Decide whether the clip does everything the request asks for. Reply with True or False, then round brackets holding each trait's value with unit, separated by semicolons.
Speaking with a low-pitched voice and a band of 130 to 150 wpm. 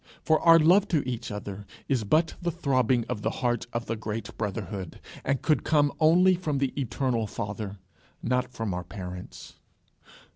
False (125 Hz; 170 wpm)